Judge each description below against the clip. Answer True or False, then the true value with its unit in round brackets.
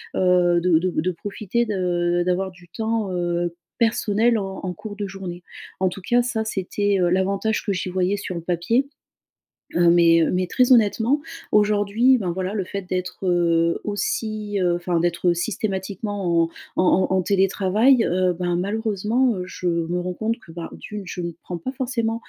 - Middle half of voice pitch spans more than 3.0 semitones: True (3.4 semitones)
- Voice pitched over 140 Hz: True (190 Hz)